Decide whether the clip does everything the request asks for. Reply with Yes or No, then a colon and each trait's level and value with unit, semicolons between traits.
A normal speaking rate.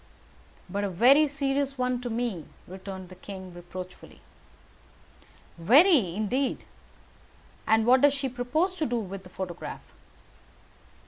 No: slow, 125 wpm